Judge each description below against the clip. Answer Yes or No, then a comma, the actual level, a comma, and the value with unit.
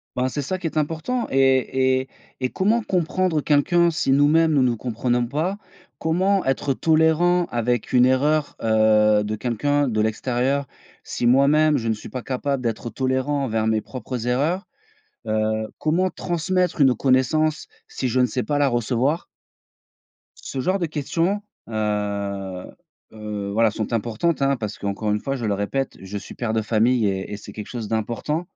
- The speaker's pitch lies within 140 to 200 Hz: No, low, 130 Hz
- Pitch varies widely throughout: Yes, wide, 5.7 semitones